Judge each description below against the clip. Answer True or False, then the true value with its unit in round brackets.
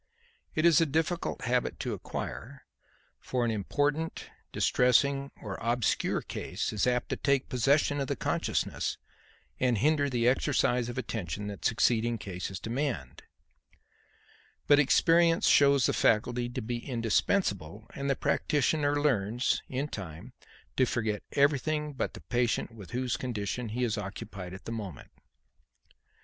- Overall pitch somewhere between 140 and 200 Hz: False (125 Hz)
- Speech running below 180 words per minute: True (140 wpm)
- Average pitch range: True (4.5 semitones)